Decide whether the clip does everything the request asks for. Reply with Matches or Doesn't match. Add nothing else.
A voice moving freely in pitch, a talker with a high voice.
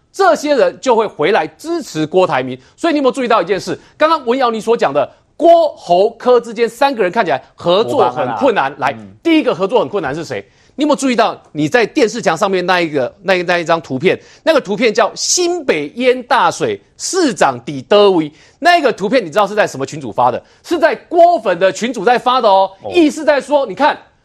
Matches